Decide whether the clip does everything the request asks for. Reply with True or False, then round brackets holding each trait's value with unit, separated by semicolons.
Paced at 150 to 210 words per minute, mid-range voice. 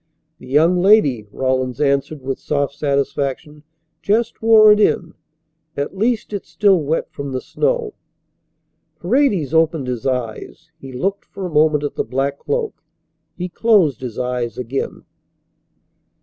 False (140 wpm; 150 Hz)